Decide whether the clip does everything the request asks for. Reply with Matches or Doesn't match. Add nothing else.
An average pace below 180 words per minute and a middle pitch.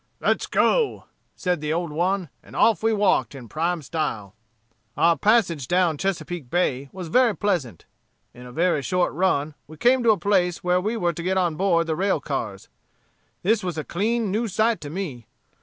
Doesn't match